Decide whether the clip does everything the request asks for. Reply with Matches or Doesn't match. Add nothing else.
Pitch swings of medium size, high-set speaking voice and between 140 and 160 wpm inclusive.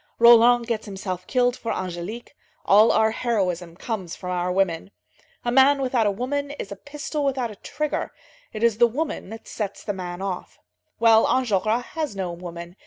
Doesn't match